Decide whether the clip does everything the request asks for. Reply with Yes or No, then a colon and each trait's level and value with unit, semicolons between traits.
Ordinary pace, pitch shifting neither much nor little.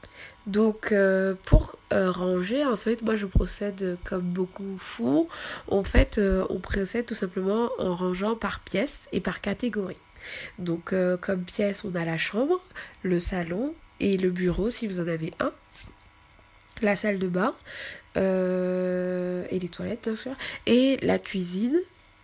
Yes: average, 160 wpm; average, 3.3 semitones